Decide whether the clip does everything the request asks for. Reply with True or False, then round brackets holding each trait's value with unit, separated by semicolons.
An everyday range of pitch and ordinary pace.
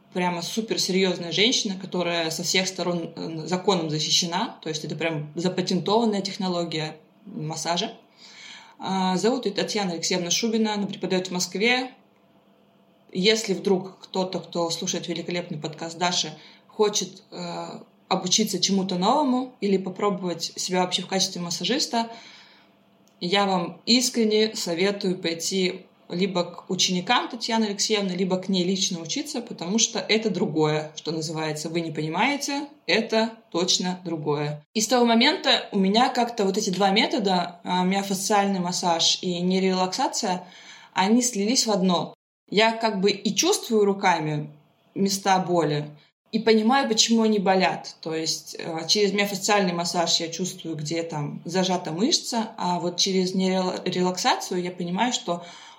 True (3.8 semitones; 135 wpm)